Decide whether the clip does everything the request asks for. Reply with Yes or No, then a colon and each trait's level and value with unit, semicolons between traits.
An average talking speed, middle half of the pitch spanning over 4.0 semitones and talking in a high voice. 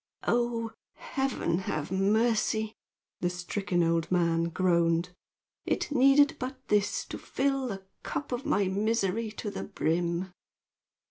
No: slow, 125 wpm; average, 5.3 semitones; high, 200 Hz